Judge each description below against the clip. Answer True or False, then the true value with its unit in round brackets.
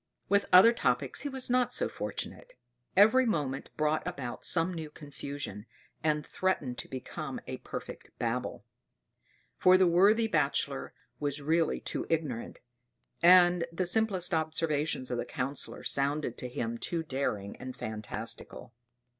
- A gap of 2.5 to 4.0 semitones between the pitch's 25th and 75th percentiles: False (5.1 semitones)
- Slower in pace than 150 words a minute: True (140 wpm)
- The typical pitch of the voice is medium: True (155 Hz)